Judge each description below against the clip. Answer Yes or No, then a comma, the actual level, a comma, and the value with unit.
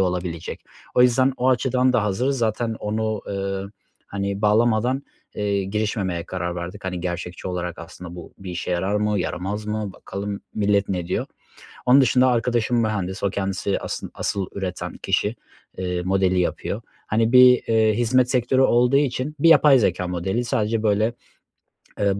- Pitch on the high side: No, low, 105 Hz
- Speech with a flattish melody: No, average, 4.3 semitones